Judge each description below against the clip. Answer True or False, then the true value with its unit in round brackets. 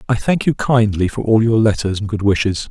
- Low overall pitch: True (110 Hz)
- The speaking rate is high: True (245 wpm)